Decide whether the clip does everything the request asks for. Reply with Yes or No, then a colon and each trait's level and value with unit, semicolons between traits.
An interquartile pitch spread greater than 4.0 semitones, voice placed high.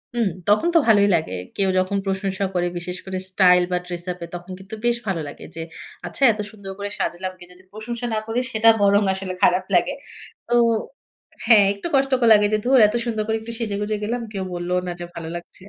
No: average, 3.3 semitones; high, 200 Hz